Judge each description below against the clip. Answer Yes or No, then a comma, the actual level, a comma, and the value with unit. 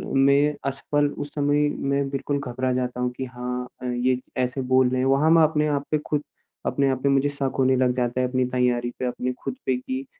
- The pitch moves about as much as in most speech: No, narrow, 2.0 semitones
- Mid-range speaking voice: No, low, 130 Hz